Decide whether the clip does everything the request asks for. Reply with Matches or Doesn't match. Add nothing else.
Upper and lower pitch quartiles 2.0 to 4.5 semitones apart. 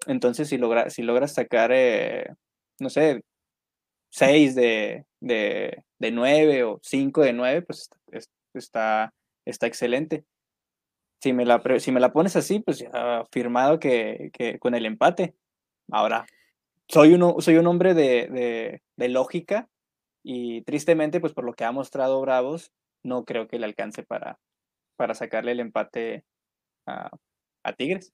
Doesn't match